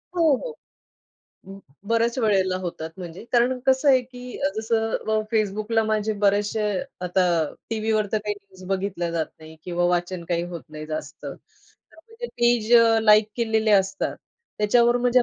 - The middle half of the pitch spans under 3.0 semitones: No, average, 4.0 semitones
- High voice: Yes, high, 215 Hz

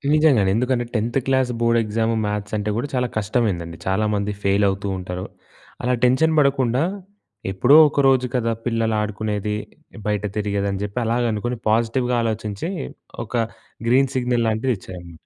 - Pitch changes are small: No, average, 3.2 semitones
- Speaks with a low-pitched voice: Yes, low, 110 Hz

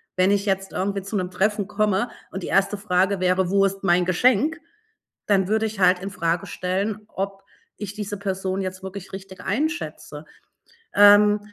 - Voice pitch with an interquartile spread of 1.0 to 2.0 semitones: Yes, narrow, 1.7 semitones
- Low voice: No, high, 195 Hz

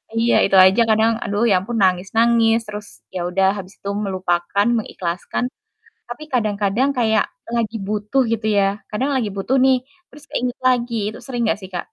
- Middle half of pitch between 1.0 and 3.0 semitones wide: No, average, 3.4 semitones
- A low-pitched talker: No, high, 215 Hz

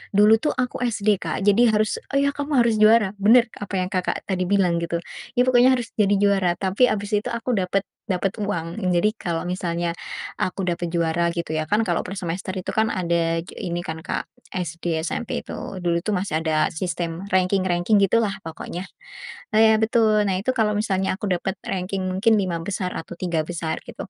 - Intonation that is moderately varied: Yes, average, 3.7 semitones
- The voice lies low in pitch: No, high, 190 Hz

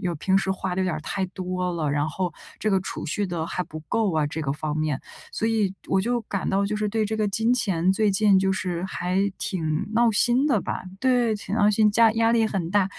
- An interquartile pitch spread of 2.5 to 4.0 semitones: Yes, average, 3.5 semitones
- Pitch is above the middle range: Yes, high, 195 Hz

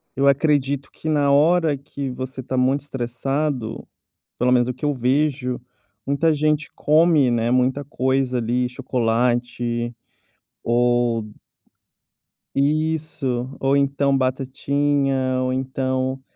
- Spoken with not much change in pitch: Yes, narrow, 2.3 semitones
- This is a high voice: No, low, 130 Hz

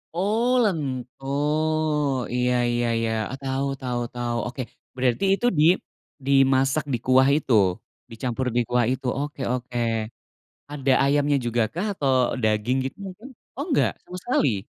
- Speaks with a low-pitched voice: Yes, low, 130 Hz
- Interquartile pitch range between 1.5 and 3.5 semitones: Yes, average, 3.1 semitones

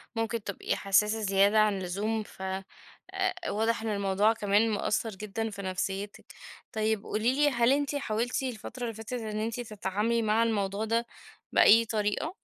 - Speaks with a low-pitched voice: No, high, 215 Hz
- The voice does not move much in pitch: Yes, narrow, 2.3 semitones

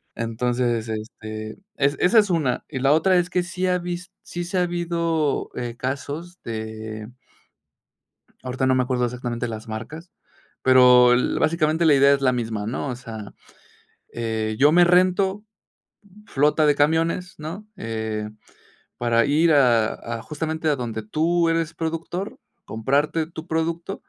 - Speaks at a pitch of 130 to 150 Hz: Yes, medium, 140 Hz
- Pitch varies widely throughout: Yes, wide, 6.0 semitones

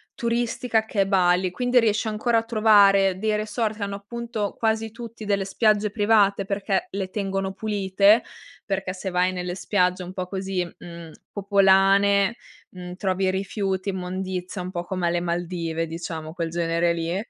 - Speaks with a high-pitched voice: Yes, high, 195 Hz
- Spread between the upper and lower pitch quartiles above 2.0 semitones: Yes, average, 2.7 semitones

